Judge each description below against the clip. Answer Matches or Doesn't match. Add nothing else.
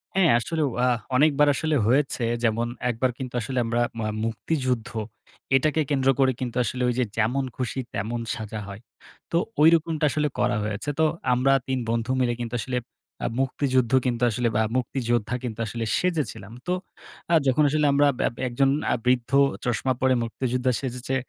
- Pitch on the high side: Doesn't match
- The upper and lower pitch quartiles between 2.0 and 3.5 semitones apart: Matches